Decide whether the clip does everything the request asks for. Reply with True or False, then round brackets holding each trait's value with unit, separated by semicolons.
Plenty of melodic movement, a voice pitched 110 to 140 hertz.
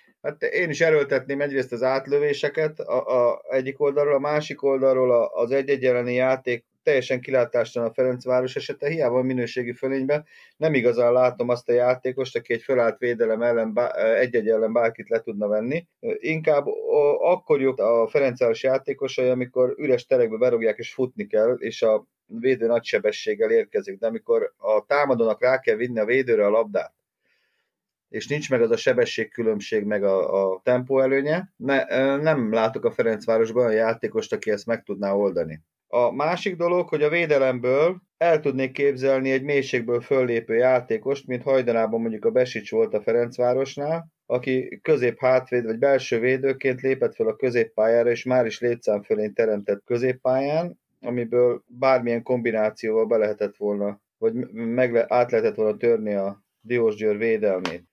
True (6.0 semitones; 130 Hz)